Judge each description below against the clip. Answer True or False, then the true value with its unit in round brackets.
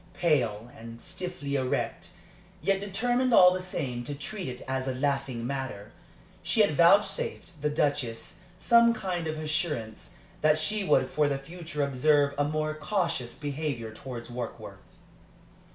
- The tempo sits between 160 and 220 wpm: False (145 wpm)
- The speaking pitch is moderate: True (150 Hz)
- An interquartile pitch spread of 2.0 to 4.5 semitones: False (5.6 semitones)